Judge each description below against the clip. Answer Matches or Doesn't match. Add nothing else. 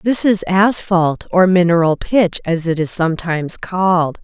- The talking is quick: Doesn't match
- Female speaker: Matches